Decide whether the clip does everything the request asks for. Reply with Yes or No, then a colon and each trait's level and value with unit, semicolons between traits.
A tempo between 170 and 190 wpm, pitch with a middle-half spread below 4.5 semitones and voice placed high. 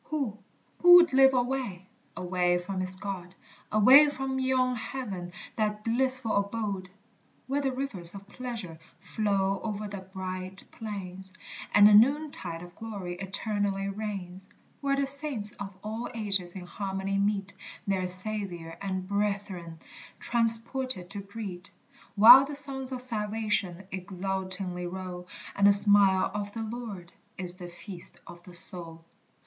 No: average, 140 wpm; average, 3.6 semitones; high, 200 Hz